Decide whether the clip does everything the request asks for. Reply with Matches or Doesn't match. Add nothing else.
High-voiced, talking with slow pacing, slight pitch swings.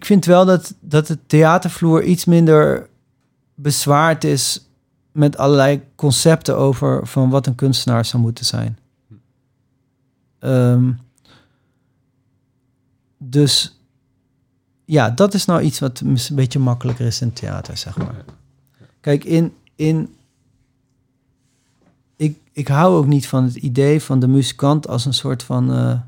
Doesn't match